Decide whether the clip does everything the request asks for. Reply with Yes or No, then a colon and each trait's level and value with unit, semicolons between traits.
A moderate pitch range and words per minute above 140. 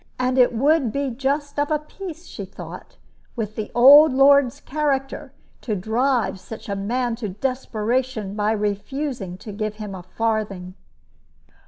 Yes: average, 4.6 semitones; average, 150 wpm